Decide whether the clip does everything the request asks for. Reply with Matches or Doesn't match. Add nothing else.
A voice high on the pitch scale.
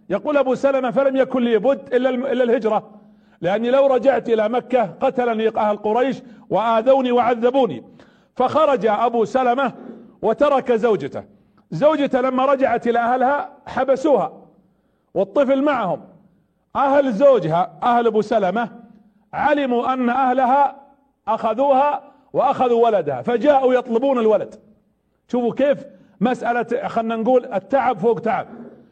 Matches